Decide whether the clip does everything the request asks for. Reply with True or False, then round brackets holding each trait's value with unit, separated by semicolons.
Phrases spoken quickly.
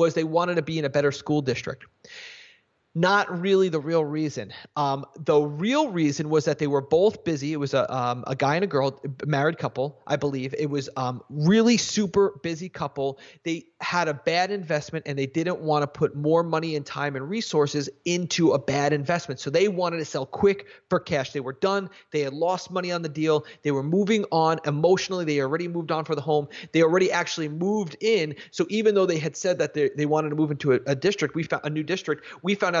True (230 wpm)